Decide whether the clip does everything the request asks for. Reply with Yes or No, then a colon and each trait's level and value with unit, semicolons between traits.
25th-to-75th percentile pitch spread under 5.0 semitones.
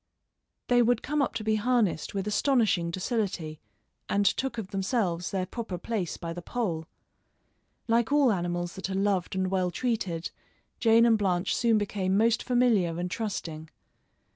Yes: average, 4.6 semitones